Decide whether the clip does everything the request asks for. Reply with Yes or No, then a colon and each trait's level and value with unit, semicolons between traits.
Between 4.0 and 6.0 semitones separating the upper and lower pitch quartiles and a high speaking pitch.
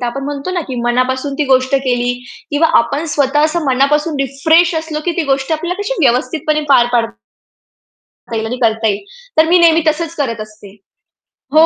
Yes: average, 4.4 semitones; very high, 275 Hz